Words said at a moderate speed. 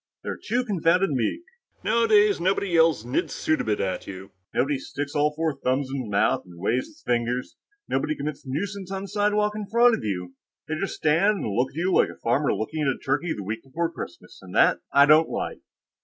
No: fast, 210 wpm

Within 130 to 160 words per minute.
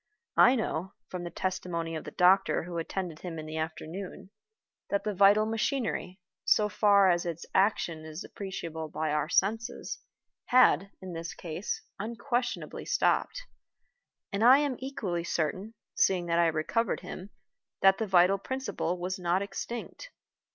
Yes: average, 150 wpm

